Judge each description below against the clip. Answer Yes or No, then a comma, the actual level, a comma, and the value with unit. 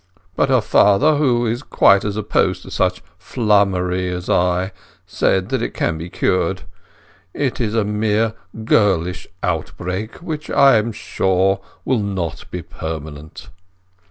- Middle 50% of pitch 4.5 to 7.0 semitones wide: No, average, 4.0 semitones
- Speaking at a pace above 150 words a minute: No, slow, 135 wpm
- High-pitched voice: No, low, 100 Hz